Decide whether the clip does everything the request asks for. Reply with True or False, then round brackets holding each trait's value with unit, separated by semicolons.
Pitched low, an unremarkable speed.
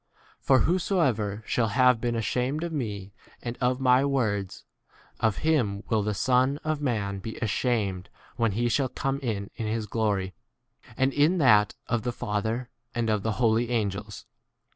True (115 Hz; 165 wpm)